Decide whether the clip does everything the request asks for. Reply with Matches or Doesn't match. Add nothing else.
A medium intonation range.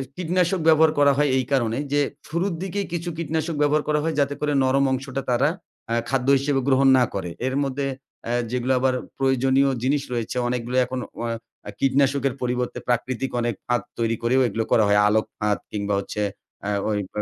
Matches